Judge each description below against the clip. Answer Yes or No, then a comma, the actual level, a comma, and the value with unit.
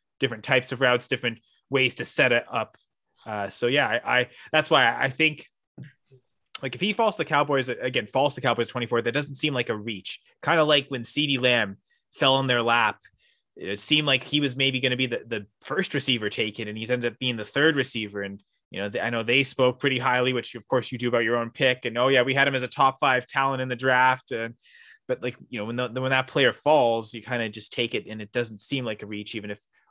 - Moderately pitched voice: No, low, 125 Hz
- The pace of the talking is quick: Yes, fast, 260 wpm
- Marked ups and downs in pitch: No, average, 2.7 semitones